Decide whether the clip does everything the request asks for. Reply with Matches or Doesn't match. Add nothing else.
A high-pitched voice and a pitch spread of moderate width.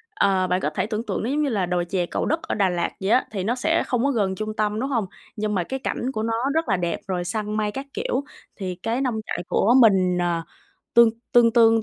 Matches